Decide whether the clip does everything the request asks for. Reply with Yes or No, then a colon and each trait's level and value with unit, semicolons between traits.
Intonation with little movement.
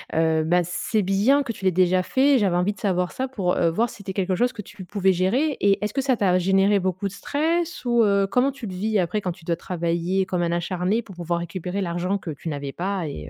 No: average, 3.2 semitones